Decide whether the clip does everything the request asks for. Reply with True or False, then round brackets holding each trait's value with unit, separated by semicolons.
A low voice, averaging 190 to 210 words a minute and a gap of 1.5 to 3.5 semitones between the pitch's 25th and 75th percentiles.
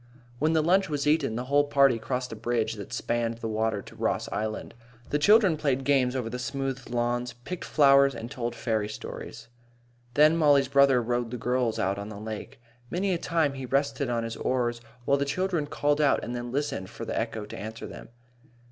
False (125 Hz; 205 wpm; 3.9 semitones)